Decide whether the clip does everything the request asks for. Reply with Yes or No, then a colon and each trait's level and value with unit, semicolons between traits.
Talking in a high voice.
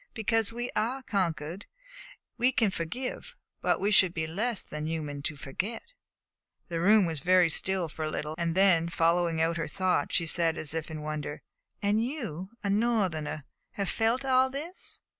No: medium, 180 Hz